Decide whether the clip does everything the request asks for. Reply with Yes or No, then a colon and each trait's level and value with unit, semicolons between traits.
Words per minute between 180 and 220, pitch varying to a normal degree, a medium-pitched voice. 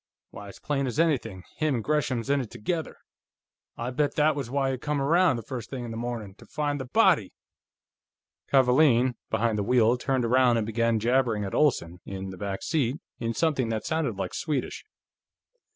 No: average, 190 wpm; average, 4.2 semitones; low, 125 Hz